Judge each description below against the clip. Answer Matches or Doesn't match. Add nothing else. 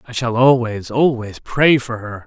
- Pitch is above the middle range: Doesn't match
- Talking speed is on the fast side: Doesn't match